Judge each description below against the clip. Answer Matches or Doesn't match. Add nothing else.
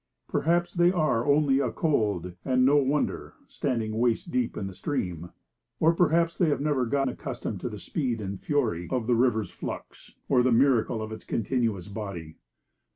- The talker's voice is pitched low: Matches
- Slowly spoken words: Doesn't match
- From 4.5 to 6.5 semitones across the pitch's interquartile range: Matches